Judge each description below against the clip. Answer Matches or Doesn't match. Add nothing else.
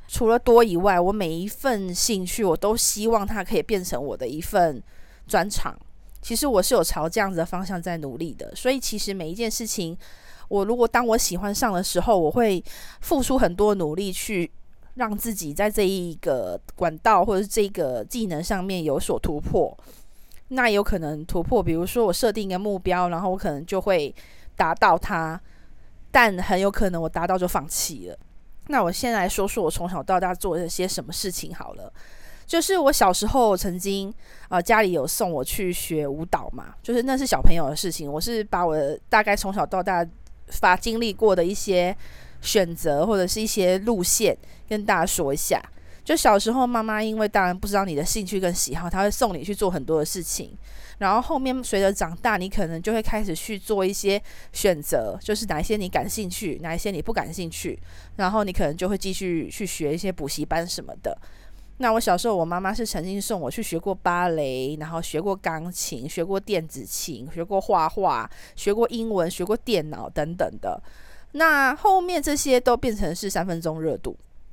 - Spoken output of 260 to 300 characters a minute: Matches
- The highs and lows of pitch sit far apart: Doesn't match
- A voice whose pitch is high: Matches